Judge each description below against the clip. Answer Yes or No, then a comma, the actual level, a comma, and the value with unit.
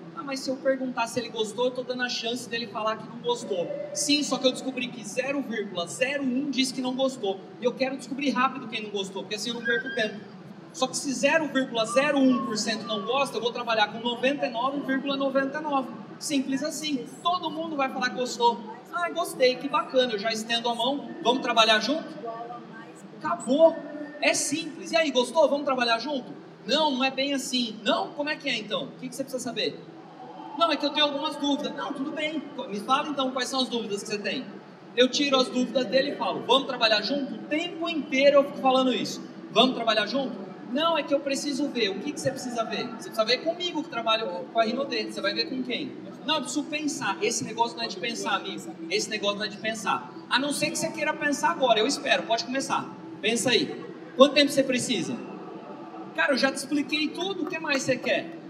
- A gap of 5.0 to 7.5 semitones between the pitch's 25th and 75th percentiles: No, average, 3.7 semitones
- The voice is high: Yes, very high, 265 Hz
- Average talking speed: No, fast, 215 wpm